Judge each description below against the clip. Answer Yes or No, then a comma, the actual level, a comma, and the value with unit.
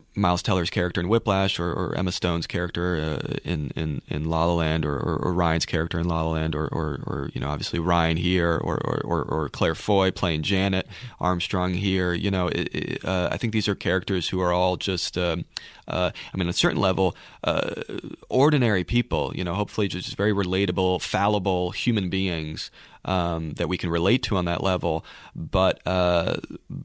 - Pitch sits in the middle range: No, very low, 90 Hz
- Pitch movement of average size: No, narrow, 2.2 semitones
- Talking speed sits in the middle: Yes, average, 195 wpm